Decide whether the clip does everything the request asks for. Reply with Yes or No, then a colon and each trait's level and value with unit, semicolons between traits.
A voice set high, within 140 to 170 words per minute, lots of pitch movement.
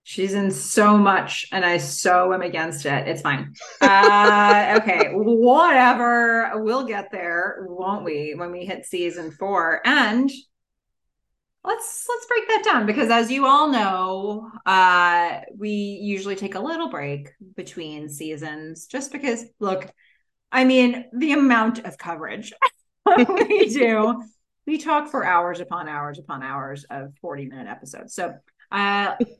Yes: high, 200 Hz; average, 145 wpm; wide, 5.9 semitones